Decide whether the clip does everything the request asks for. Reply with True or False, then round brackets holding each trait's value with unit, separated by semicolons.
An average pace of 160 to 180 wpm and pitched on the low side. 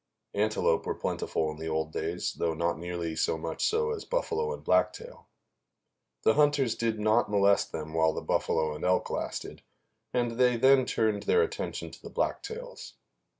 True (170 wpm; 110 Hz)